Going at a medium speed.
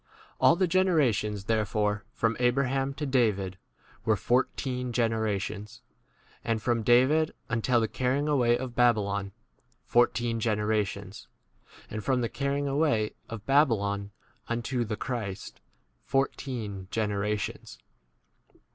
No: slow, 110 wpm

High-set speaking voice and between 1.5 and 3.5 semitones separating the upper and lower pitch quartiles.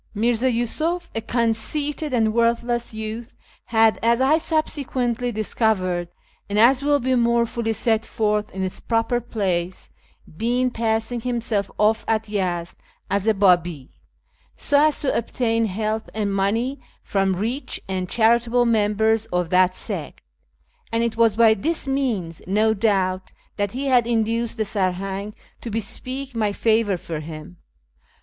Yes: high, 225 Hz; average, 3.1 semitones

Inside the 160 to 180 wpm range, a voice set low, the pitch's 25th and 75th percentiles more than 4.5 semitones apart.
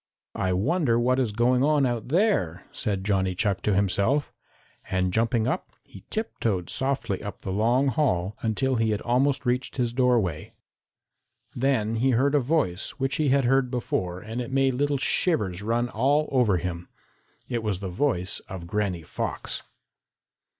Yes: average, 165 wpm; low, 115 Hz; wide, 5.5 semitones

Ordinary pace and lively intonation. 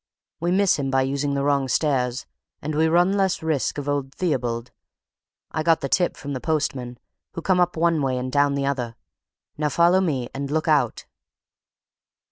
No: average, 185 wpm; average, 3.6 semitones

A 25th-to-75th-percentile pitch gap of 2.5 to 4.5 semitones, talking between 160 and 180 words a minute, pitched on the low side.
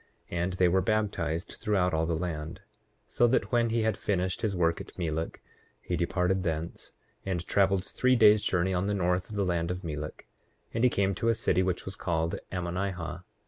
No: average, 2.8 semitones; average, 200 wpm; very low, 90 Hz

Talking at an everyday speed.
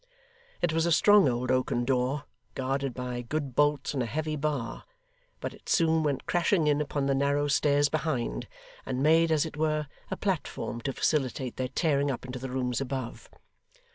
Yes: average, 180 wpm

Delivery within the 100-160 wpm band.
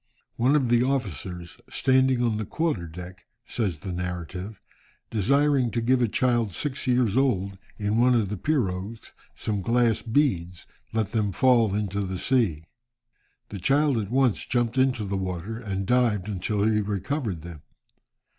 Yes: average, 155 wpm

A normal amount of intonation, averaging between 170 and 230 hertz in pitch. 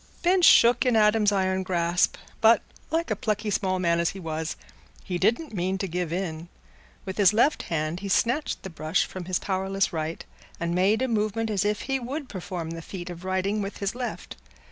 Yes: average, 4.0 semitones; high, 190 Hz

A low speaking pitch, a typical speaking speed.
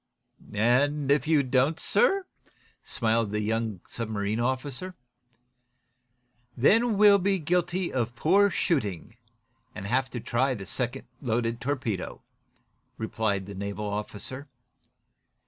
No: low, 125 Hz; slow, 115 wpm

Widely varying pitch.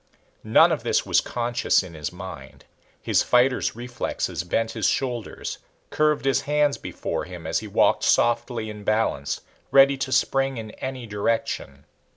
Yes: wide, 5.9 semitones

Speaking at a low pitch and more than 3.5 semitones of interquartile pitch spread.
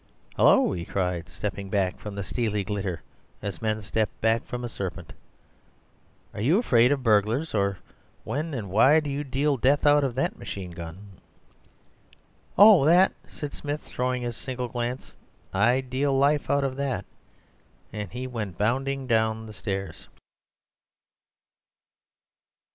Yes: low, 120 Hz; average, 5.3 semitones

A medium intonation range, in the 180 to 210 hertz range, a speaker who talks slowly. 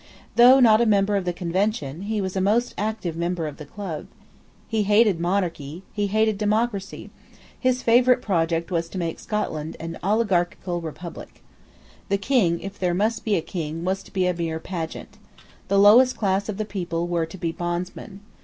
No: average, 3.9 semitones; high, 190 Hz; average, 180 wpm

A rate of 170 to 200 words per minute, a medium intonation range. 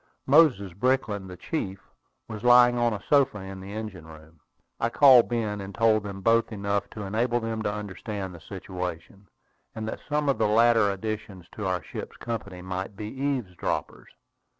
Yes: average, 175 wpm; average, 3.4 semitones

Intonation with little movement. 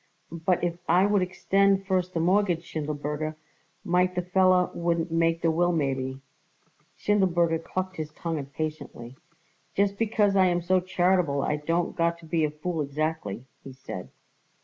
No: average, 3.0 semitones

